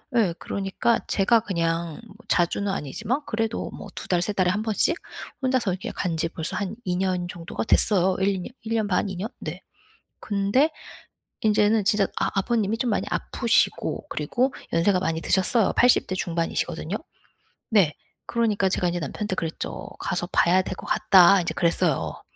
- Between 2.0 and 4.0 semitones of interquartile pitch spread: Yes, average, 3.7 semitones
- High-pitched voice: Yes, high, 195 Hz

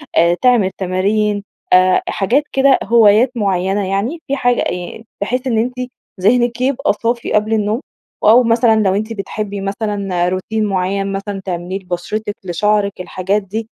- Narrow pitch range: No, average, 3.2 semitones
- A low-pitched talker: No, high, 205 Hz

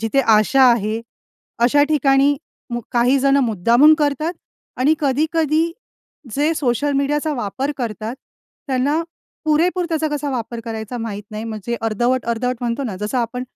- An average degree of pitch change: Yes, average, 4.2 semitones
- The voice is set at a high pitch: Yes, very high, 255 Hz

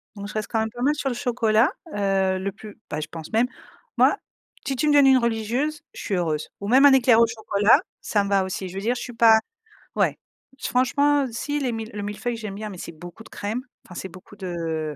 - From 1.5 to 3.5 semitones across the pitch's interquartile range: No, average, 4.1 semitones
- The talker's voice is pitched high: Yes, high, 220 Hz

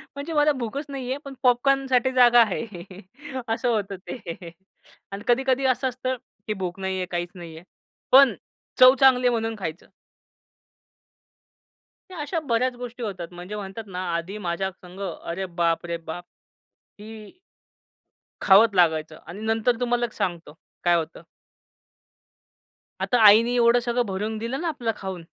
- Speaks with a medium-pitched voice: No, high, 220 Hz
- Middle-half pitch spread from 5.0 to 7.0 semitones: Yes, average, 5.3 semitones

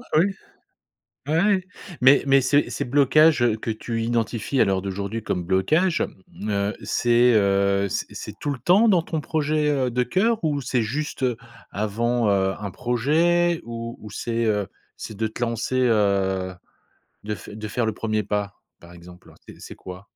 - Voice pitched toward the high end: No, low, 115 Hz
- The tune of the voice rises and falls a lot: Yes, wide, 5.9 semitones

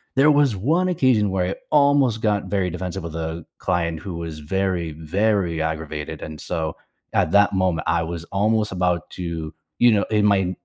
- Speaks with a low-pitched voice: Yes, very low, 90 Hz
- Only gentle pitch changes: No, average, 4.2 semitones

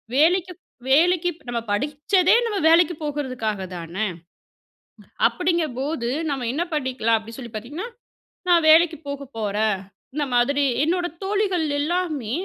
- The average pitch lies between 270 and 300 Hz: Yes, very high, 290 Hz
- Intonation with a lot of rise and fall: Yes, wide, 6.3 semitones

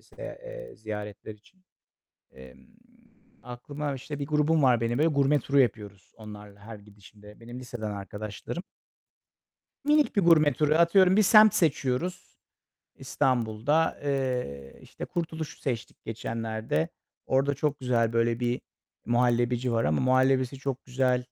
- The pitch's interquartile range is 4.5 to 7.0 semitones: Yes, average, 5.0 semitones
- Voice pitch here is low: Yes, low, 125 Hz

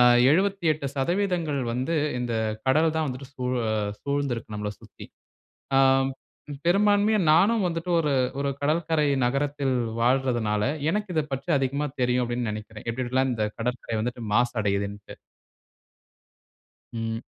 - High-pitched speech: No, low, 135 Hz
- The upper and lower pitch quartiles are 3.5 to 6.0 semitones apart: Yes, average, 5.0 semitones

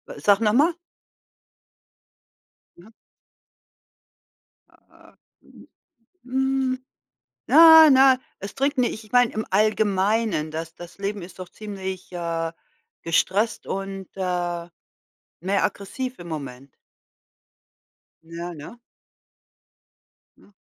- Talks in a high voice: Yes, high, 195 Hz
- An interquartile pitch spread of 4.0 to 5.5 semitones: Yes, average, 5.1 semitones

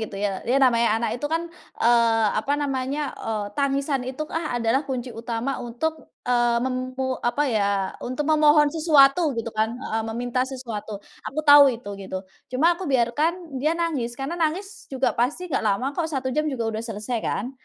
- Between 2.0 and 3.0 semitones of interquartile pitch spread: No, average, 4.0 semitones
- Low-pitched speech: No, very high, 255 Hz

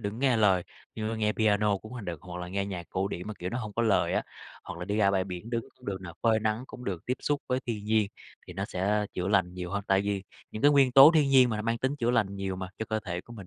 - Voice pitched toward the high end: No, low, 105 Hz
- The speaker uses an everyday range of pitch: Yes, average, 3.4 semitones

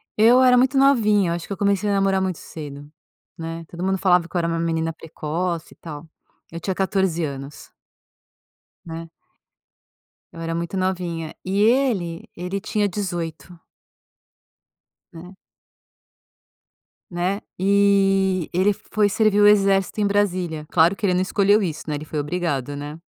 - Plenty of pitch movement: No, average, 3.3 semitones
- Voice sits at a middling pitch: Yes, medium, 180 Hz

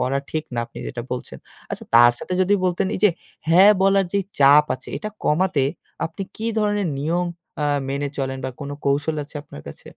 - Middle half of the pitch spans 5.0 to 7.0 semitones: Yes, wide, 5.5 semitones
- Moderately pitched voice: Yes, medium, 150 Hz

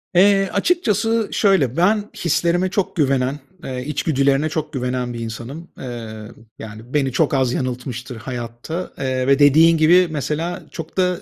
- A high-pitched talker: No, medium, 145 Hz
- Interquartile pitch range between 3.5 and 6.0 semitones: Yes, wide, 5.6 semitones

